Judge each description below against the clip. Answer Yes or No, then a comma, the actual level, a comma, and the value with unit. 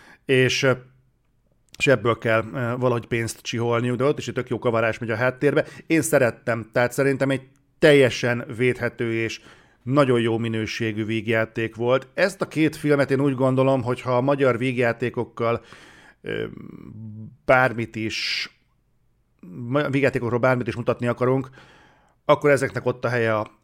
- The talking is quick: No, average, 140 wpm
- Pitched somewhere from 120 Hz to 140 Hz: Yes, low, 125 Hz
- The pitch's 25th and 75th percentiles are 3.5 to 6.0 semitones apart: No, narrow, 2.5 semitones